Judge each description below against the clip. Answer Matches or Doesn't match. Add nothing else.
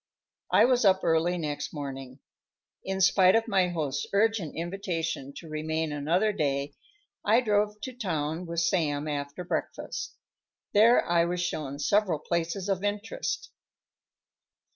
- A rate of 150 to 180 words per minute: Doesn't match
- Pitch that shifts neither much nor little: Matches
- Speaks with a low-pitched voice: Doesn't match